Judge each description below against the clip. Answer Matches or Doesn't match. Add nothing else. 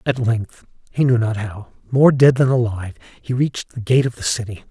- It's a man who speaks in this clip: Matches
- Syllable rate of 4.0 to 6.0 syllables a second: Matches